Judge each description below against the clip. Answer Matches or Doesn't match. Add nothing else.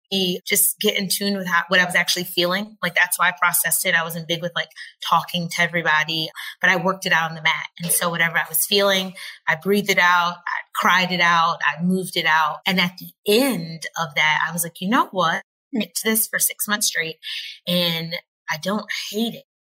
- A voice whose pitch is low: Doesn't match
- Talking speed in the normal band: Doesn't match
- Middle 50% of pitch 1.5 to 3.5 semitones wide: Matches